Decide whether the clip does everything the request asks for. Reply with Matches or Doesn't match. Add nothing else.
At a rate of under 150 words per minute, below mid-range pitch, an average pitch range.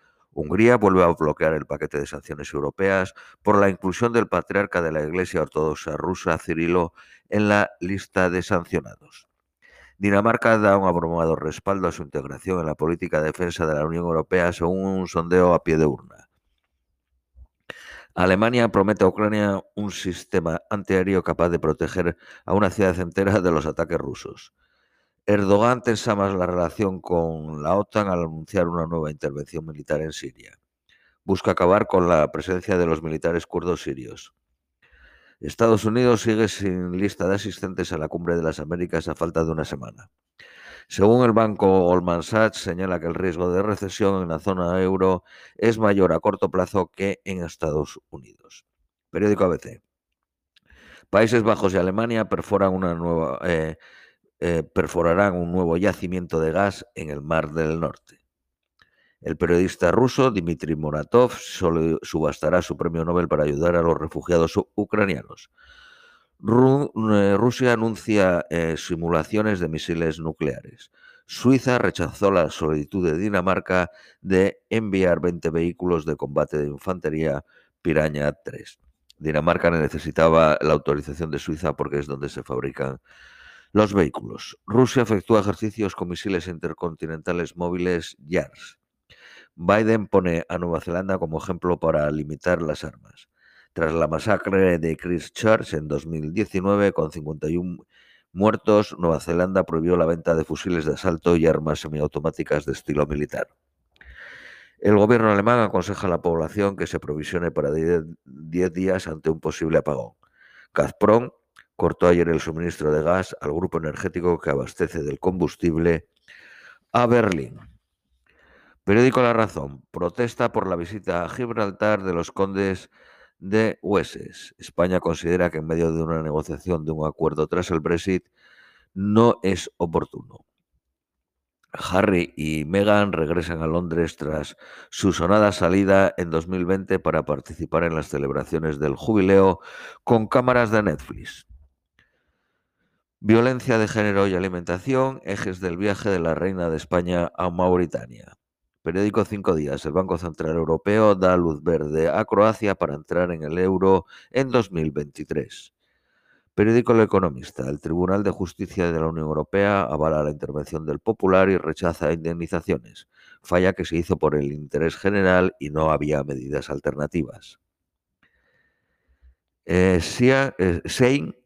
Matches